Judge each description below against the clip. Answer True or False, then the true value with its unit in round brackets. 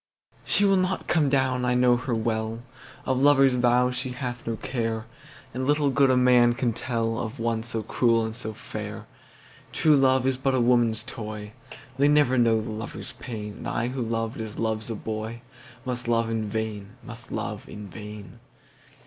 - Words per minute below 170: True (160 wpm)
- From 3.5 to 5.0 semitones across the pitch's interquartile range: False (2.5 semitones)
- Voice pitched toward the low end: True (120 Hz)